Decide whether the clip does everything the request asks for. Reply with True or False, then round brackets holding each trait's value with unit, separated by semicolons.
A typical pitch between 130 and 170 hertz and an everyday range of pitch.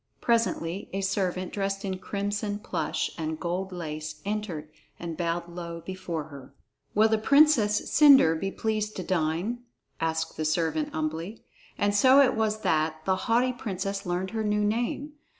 False (190 Hz; 4.5 semitones)